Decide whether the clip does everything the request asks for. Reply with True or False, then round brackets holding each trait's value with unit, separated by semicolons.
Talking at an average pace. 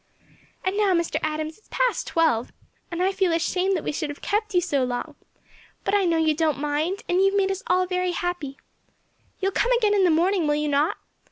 False (230 wpm)